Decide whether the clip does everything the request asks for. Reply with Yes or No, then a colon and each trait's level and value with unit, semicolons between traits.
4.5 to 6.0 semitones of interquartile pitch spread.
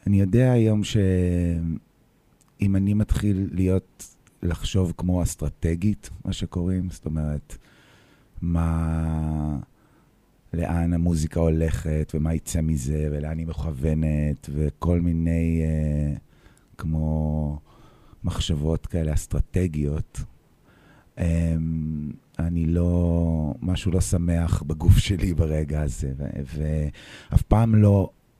No: average, 3.0 semitones